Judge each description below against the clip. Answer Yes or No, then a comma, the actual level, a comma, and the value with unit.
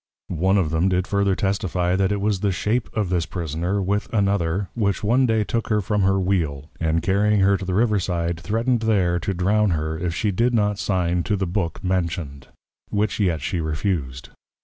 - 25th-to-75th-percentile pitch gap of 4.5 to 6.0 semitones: No, average, 3.2 semitones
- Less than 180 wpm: No, average, 195 wpm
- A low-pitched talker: Yes, very low, 95 Hz